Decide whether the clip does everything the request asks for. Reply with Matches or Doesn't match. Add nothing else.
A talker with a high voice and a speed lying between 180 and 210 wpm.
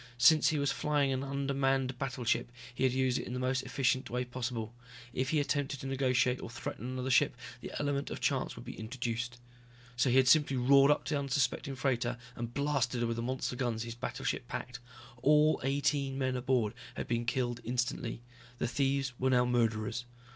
Doesn't match